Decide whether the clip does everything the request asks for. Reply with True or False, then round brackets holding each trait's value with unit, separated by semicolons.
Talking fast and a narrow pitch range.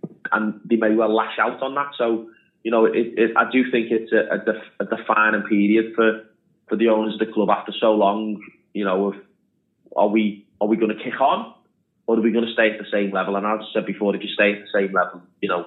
True (255 wpm; 1.7 semitones)